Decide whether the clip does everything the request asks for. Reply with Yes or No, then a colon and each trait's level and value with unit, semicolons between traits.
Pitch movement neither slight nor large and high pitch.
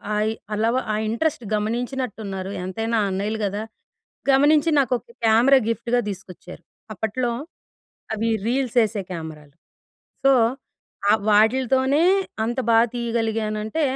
Yes: average, 3.3 semitones; high, 225 Hz